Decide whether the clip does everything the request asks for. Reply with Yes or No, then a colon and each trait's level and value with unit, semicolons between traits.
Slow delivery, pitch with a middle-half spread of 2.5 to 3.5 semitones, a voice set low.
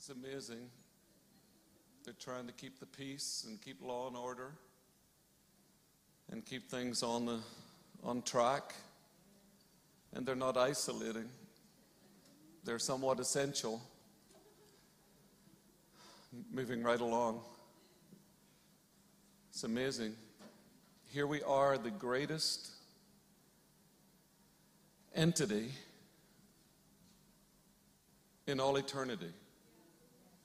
Yes: slow, 80 wpm; average, 3.0 semitones; low, 130 Hz